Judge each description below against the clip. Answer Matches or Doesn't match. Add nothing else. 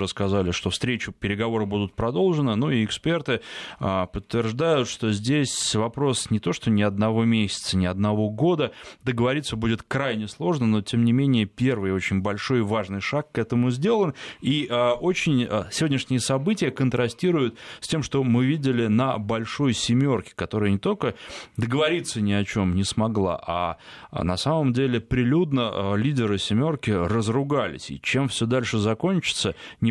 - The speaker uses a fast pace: Matches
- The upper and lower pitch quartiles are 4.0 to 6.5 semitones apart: Matches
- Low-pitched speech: Matches